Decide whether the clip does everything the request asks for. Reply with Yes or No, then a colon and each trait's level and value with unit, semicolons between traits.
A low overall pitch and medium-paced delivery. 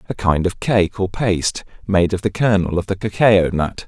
No: very low, 95 Hz; fast, 215 wpm